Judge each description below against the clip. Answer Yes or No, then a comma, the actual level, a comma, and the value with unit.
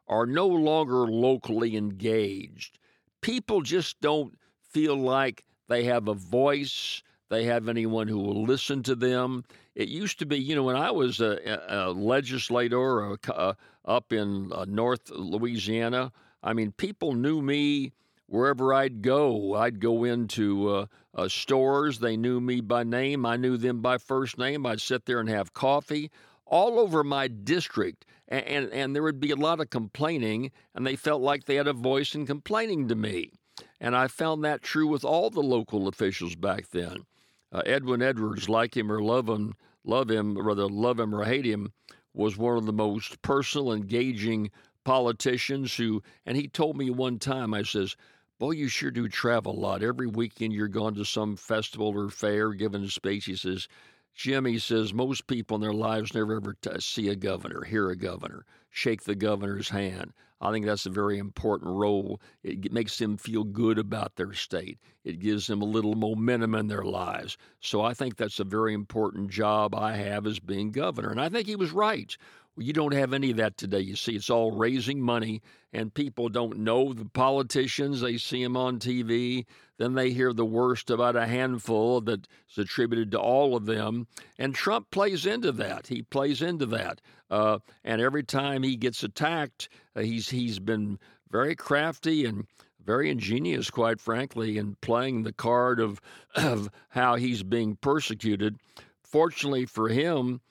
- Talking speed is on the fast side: No, average, 180 wpm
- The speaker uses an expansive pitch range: No, average, 3.8 semitones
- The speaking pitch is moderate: No, low, 120 Hz